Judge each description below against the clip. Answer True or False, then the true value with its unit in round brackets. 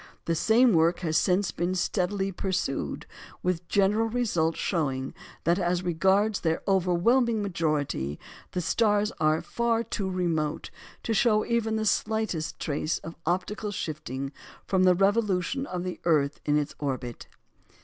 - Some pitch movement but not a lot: True (4.6 semitones)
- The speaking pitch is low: False (180 Hz)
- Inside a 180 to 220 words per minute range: False (150 wpm)